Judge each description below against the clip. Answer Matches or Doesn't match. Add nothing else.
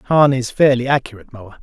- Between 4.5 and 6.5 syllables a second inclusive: Matches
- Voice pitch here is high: Doesn't match